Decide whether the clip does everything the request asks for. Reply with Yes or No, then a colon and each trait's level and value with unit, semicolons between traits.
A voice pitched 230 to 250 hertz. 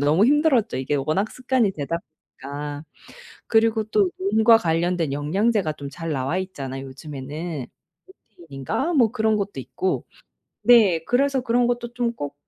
No: medium, 185 Hz